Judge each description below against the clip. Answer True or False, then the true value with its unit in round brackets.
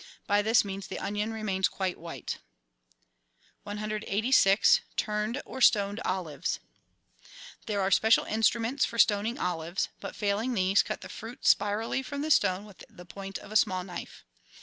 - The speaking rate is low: False (150 wpm)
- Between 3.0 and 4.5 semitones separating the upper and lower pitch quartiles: False (2.6 semitones)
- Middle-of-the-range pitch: False (205 Hz)